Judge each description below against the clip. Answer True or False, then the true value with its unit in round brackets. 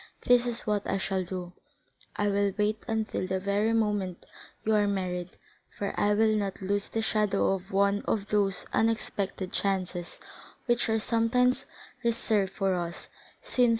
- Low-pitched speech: False (205 Hz)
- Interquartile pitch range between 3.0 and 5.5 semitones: False (2.5 semitones)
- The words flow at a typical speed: True (160 wpm)